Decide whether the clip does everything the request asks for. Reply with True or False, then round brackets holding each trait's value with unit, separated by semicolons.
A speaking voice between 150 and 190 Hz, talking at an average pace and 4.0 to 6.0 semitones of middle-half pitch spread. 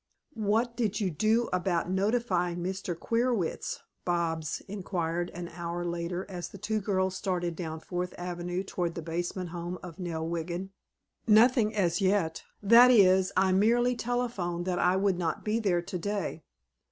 False (185 Hz; 155 wpm; 3.2 semitones)